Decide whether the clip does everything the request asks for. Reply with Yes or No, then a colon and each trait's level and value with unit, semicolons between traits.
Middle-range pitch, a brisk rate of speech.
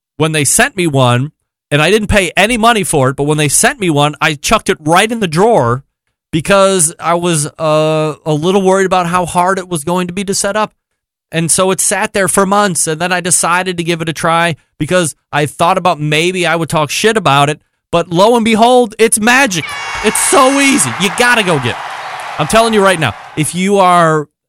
Yes: medium, 175 Hz; fast, 230 wpm